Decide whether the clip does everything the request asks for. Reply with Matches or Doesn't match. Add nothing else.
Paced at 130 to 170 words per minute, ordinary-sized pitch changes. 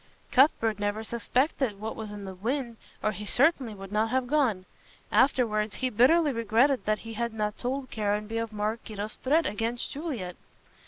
Matches